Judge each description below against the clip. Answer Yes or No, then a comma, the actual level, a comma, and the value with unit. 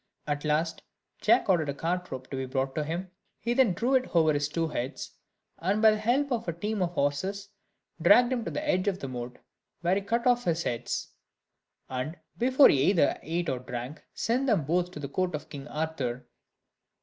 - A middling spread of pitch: No, wide, 6.6 semitones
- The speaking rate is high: Yes, fast, 210 wpm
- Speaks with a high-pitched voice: No, medium, 170 Hz